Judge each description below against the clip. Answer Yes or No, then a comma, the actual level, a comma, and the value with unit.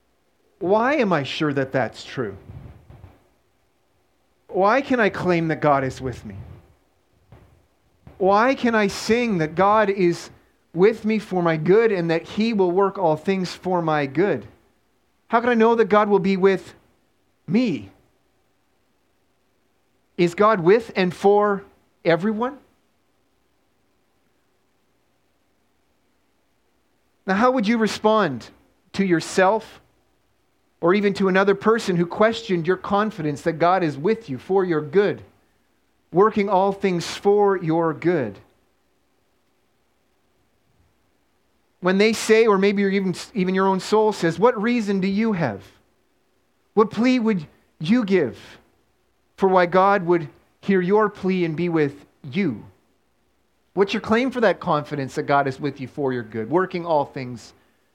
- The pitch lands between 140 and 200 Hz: Yes, medium, 185 Hz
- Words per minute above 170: No, slow, 135 wpm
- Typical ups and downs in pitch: No, wide, 6.0 semitones